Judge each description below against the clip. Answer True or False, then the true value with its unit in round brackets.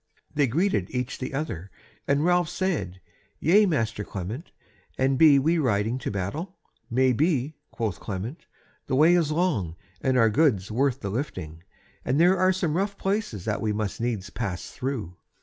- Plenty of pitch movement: True (7.3 semitones)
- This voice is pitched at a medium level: False (130 Hz)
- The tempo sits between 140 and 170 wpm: True (165 wpm)